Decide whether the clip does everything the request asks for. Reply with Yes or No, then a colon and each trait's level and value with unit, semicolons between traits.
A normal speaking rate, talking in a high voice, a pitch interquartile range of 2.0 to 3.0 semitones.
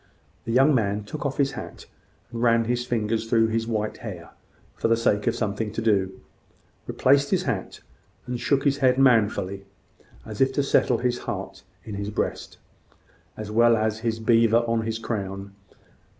No: average, 175 wpm; low, 115 Hz; narrow, 2.6 semitones